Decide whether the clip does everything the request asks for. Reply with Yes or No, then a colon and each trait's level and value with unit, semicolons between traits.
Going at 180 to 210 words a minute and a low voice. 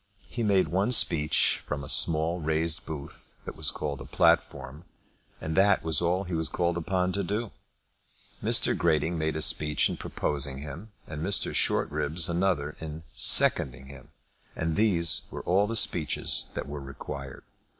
No: average, 165 wpm; very low, 80 Hz